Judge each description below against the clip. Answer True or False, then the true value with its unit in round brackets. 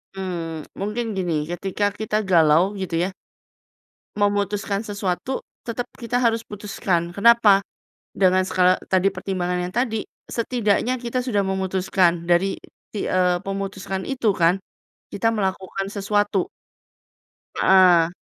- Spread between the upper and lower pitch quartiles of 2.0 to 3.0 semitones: True (2.5 semitones)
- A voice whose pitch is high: True (195 Hz)